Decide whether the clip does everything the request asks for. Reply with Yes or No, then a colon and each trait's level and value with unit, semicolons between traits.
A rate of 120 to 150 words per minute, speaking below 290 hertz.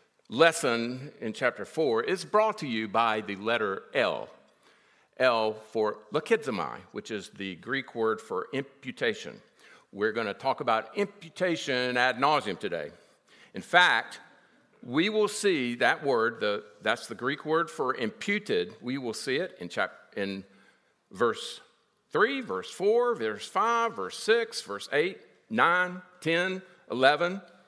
Yes: average, 140 wpm; medium, 140 Hz